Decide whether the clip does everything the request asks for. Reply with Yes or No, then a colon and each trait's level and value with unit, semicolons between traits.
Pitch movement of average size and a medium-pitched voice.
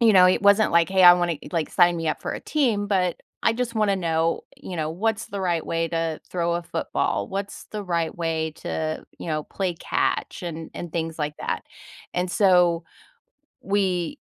Yes: average, 3.1 semitones; medium, 175 Hz